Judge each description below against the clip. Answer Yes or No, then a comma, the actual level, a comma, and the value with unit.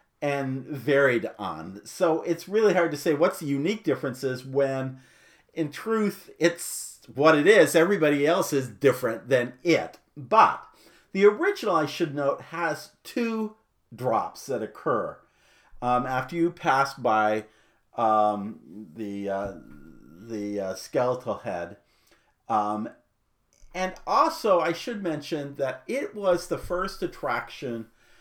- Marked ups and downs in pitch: Yes, wide, 6.4 semitones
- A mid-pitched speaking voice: Yes, medium, 145 Hz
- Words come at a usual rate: No, slow, 130 wpm